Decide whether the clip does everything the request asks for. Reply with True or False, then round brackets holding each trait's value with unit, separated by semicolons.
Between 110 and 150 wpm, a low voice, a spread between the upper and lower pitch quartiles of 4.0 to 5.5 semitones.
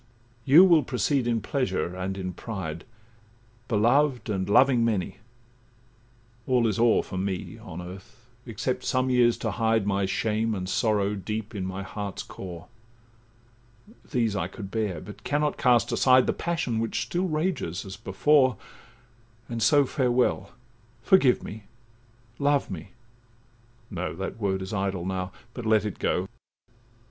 True (135 wpm; 115 Hz; 4.4 semitones)